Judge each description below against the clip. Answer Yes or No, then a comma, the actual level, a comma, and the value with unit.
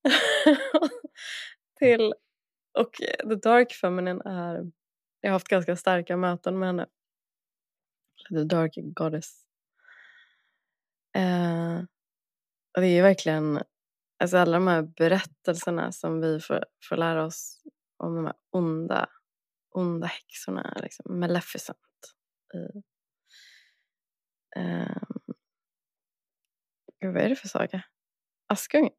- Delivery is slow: Yes, slow, 105 wpm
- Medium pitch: Yes, medium, 180 Hz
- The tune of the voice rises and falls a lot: No, average, 4.7 semitones